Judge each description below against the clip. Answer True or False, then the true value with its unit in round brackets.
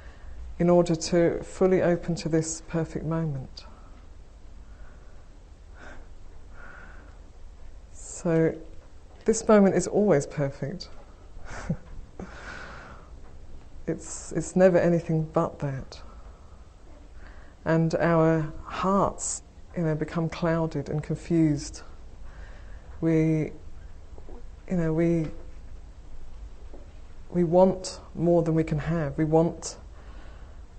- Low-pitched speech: True (120 Hz)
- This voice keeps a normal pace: False (85 wpm)